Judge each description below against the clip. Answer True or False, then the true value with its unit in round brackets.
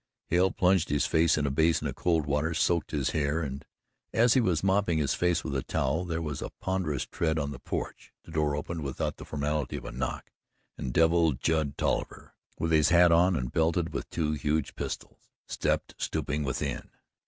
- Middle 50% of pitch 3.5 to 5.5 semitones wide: False (2.9 semitones)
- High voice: False (80 Hz)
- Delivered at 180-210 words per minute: True (200 wpm)